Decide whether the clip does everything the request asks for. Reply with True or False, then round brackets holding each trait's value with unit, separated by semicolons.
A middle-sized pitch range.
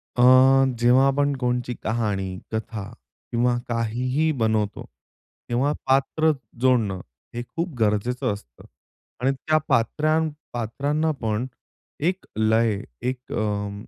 True (3.8 semitones)